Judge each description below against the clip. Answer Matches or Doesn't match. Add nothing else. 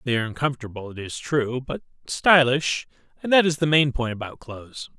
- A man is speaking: Matches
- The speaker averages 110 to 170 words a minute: Doesn't match